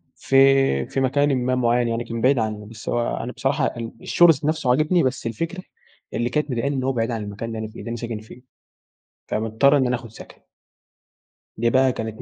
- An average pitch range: Yes, average, 3.0 semitones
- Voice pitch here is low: Yes, low, 125 Hz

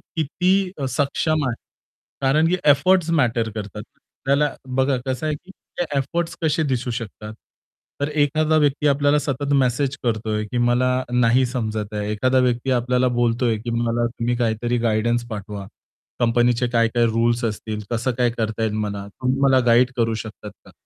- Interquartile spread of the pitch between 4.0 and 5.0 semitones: No, average, 3.5 semitones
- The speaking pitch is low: Yes, low, 120 Hz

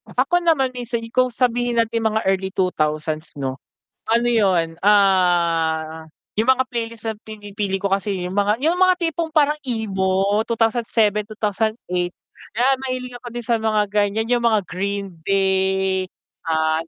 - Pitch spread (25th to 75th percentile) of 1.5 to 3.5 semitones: No, average, 4.1 semitones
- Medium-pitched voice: No, high, 210 Hz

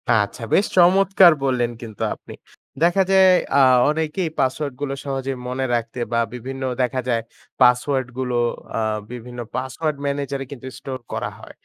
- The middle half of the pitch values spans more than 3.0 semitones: Yes, average, 3.5 semitones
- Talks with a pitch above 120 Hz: Yes, low, 135 Hz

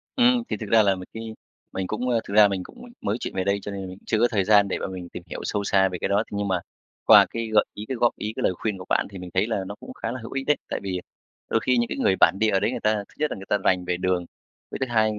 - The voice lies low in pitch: Yes, low, 105 Hz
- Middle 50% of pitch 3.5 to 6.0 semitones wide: No, average, 3.1 semitones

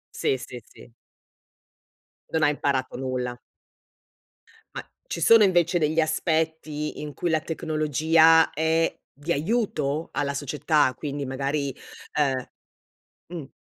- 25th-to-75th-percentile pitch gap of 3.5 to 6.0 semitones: No, narrow, 2.5 semitones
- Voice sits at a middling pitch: Yes, medium, 155 Hz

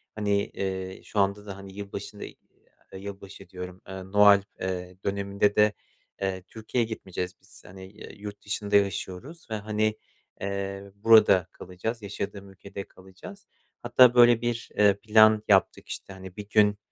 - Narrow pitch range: Yes, narrow, 1.8 semitones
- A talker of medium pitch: No, low, 100 Hz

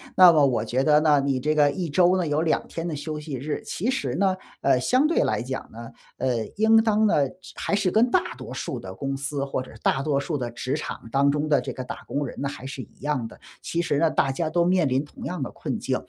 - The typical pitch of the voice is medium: Yes, medium, 145 Hz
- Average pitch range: Yes, average, 4.3 semitones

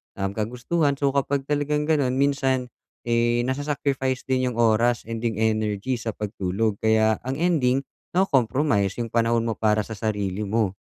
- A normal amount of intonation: Yes, average, 3.9 semitones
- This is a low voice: Yes, low, 120 Hz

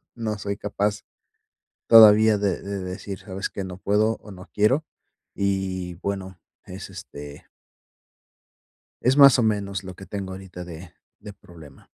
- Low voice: Yes, low, 100 Hz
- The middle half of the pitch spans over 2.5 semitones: No, narrow, 2.1 semitones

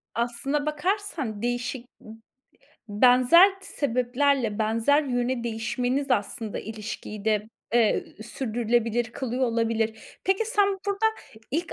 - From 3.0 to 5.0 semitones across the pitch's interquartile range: Yes, average, 4.3 semitones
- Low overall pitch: No, high, 245 Hz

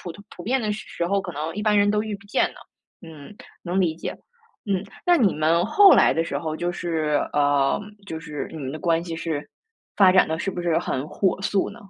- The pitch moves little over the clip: No, average, 4.2 semitones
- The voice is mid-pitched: Yes, medium, 175 Hz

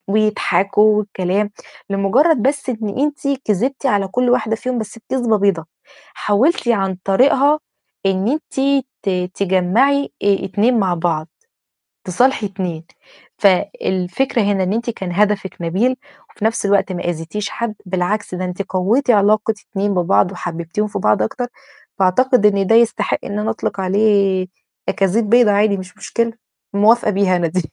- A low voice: No, high, 205 Hz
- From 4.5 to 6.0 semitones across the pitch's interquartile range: No, average, 3.7 semitones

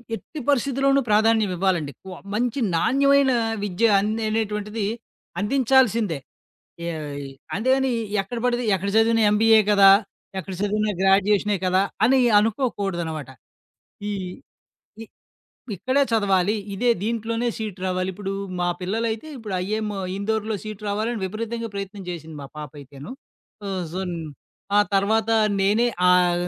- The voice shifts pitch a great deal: No, average, 3.3 semitones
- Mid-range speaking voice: No, high, 210 Hz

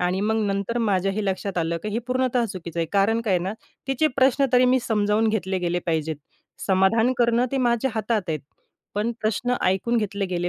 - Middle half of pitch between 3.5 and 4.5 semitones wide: Yes, average, 3.9 semitones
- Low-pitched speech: No, high, 210 Hz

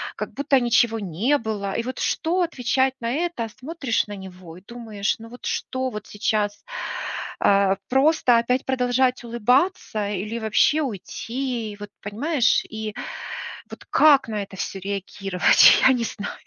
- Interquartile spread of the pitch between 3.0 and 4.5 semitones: Yes, average, 4.1 semitones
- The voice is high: Yes, high, 230 Hz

